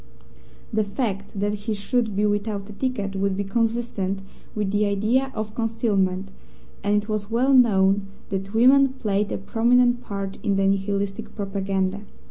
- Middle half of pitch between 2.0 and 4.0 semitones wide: Yes, narrow, 2.5 semitones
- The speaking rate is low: No, average, 155 wpm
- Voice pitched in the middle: No, high, 205 Hz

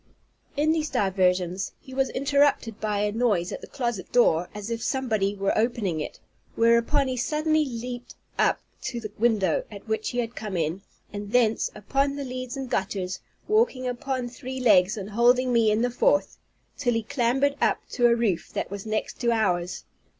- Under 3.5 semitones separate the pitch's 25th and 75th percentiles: No, average, 4.1 semitones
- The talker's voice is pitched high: Yes, high, 235 Hz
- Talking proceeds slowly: No, average, 185 wpm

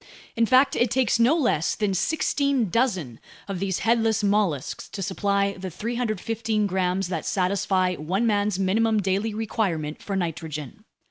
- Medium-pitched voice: No, high, 200 Hz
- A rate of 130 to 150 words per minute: Yes, average, 145 wpm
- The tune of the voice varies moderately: Yes, average, 3.6 semitones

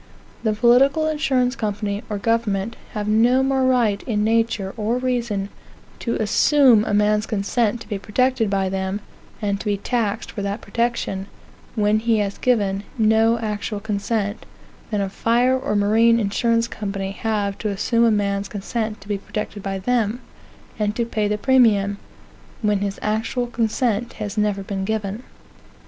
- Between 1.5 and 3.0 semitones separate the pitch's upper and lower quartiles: Yes, narrow, 2.5 semitones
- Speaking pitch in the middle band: No, high, 215 Hz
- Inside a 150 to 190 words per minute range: Yes, average, 160 wpm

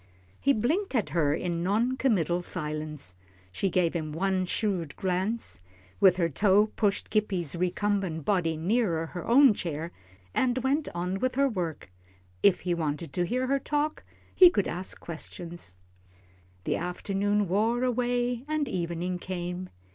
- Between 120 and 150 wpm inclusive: Yes, average, 145 wpm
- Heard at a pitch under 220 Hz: Yes, medium, 185 Hz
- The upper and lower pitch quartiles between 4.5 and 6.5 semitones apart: Yes, wide, 5.4 semitones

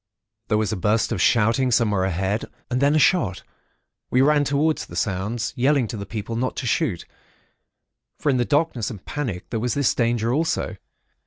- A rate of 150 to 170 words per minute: No, average, 185 wpm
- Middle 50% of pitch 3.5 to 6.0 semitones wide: Yes, average, 4.8 semitones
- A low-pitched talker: Yes, low, 120 Hz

